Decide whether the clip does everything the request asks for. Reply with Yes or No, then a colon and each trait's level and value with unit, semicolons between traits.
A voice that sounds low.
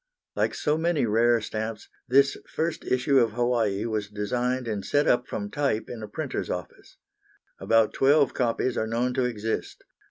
Yes: low, 120 Hz